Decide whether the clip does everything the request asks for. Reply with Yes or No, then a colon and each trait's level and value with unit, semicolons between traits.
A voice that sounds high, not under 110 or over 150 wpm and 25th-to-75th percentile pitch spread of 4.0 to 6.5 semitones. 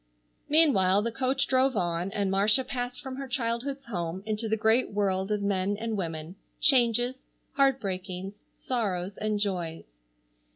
Yes: high, 210 Hz; average, 140 wpm; average, 4.9 semitones